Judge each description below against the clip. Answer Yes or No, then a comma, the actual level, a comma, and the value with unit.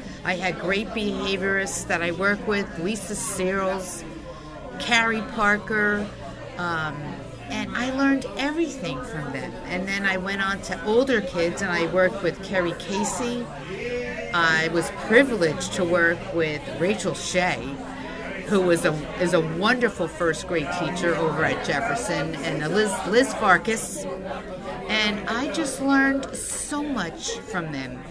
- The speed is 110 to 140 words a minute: Yes, slow, 135 wpm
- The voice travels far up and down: No, average, 4.0 semitones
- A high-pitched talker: Yes, high, 195 Hz